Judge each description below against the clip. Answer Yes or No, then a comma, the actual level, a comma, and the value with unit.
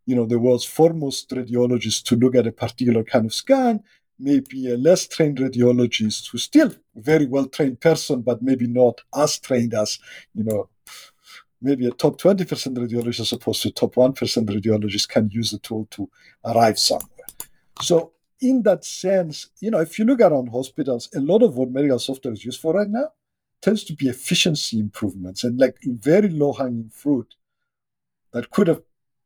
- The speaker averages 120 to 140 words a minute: No, average, 175 wpm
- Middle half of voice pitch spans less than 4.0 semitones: No, average, 5.1 semitones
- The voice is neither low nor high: No, low, 130 Hz